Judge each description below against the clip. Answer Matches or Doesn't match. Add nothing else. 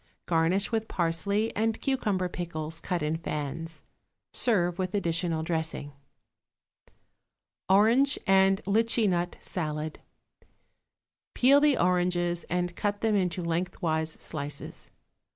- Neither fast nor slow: Doesn't match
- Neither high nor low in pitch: Matches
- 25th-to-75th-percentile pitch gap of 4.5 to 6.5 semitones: Doesn't match